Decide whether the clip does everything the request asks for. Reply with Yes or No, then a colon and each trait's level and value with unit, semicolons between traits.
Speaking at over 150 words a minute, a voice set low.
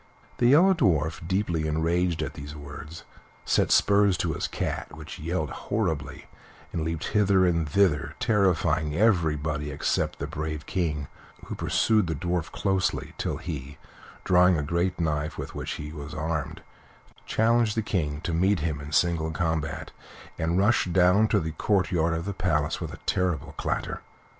Yes: average, 160 wpm; very low, 85 Hz